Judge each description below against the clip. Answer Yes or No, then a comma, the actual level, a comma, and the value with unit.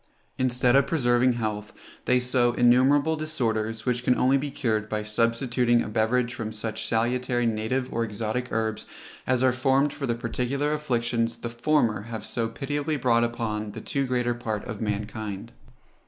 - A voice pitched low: Yes, low, 120 Hz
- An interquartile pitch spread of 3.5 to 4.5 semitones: No, narrow, 2.4 semitones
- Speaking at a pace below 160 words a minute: No, average, 165 wpm